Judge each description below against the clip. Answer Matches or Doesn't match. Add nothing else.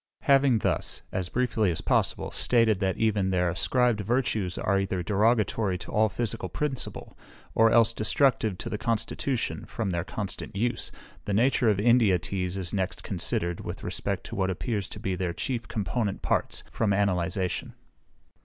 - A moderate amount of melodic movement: Matches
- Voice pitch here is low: Matches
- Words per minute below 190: Matches